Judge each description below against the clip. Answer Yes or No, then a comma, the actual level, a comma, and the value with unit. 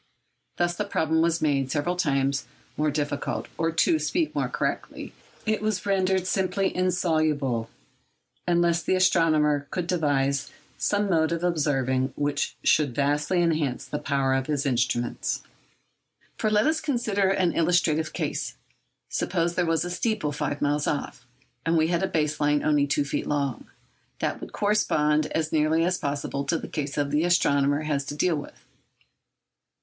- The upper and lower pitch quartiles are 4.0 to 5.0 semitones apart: No, average, 3.6 semitones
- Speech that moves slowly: No, average, 155 wpm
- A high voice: No, medium, 155 Hz